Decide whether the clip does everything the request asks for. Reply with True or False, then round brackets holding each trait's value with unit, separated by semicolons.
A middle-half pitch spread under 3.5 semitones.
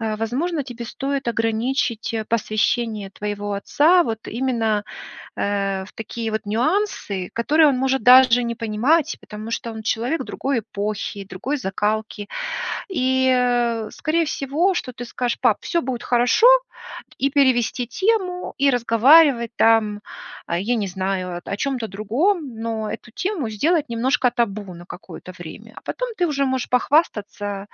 False (4.3 semitones)